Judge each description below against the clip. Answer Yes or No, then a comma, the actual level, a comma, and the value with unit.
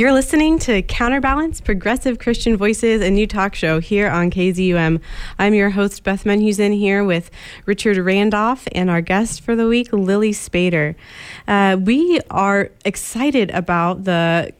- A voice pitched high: Yes, high, 205 Hz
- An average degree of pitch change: Yes, average, 3.7 semitones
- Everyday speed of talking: Yes, average, 150 wpm